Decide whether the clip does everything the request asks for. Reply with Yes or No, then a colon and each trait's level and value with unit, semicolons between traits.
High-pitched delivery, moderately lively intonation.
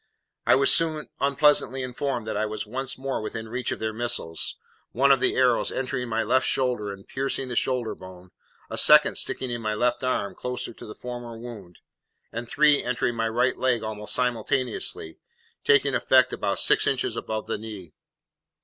No: low, 120 Hz; average, 3.0 semitones